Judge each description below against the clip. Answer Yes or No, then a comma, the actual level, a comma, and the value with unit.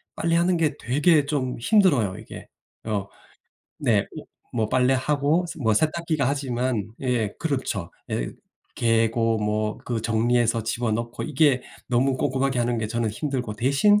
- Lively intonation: No, average, 4.1 semitones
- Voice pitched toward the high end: No, low, 125 Hz